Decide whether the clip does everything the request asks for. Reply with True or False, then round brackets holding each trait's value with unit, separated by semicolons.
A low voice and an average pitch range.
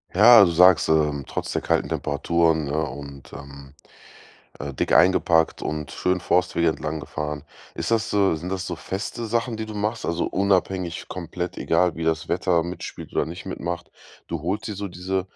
True (85 Hz; 3.5 semitones)